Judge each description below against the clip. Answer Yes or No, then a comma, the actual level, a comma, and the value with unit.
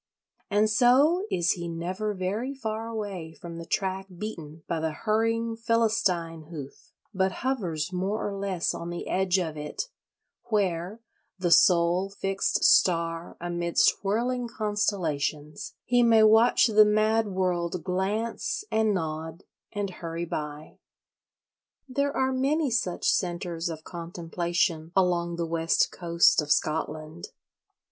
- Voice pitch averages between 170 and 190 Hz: Yes, medium, 185 Hz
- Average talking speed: No, slow, 130 wpm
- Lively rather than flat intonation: No, average, 4.4 semitones